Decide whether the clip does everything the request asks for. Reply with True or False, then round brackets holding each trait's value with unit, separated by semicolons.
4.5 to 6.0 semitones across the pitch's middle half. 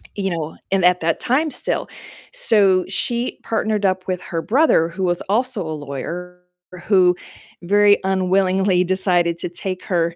False (2.6 semitones)